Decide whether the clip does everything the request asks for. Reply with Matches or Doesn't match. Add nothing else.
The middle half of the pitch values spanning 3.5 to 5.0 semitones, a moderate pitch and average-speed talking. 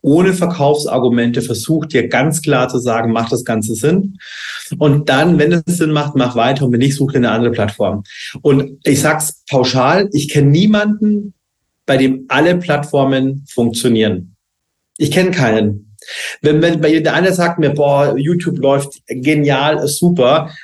Matches